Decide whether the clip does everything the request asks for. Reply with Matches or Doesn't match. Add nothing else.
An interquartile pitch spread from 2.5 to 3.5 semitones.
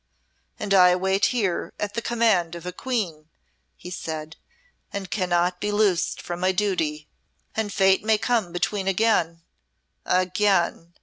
Matches